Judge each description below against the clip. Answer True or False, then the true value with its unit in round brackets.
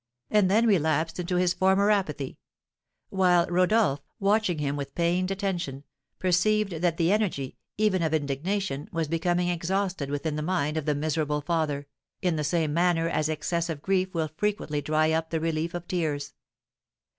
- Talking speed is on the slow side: False (165 wpm)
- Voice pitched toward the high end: False (170 Hz)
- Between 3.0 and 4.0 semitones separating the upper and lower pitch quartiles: True (3.4 semitones)